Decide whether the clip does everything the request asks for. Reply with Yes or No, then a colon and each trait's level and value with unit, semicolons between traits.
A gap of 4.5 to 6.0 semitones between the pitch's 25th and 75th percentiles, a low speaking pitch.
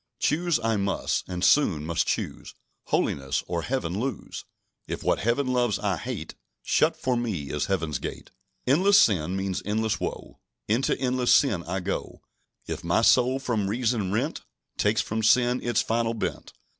Yes: average, 5.0 semitones; low, 110 Hz